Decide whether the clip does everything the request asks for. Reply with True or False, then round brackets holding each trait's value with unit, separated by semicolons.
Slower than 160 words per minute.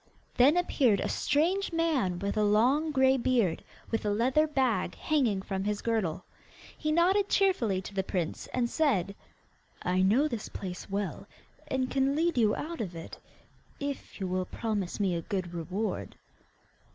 False (165 wpm)